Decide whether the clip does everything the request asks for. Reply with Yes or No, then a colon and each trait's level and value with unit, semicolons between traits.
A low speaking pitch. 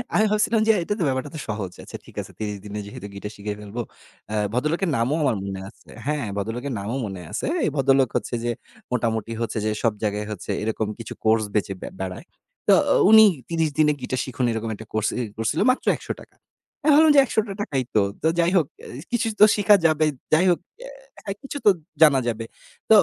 Yes: low, 125 Hz